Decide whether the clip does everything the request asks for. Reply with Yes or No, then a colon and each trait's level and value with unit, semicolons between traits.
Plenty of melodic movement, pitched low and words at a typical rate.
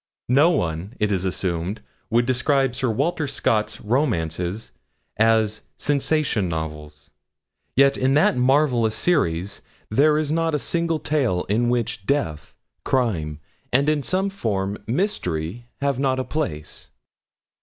No: wide, 6.9 semitones; low, 120 Hz; slow, 130 wpm